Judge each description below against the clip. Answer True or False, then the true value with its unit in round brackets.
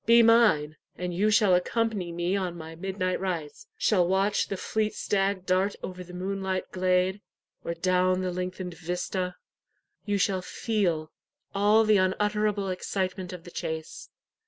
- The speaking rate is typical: True (150 wpm)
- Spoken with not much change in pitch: True (2.1 semitones)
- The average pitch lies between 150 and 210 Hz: True (185 Hz)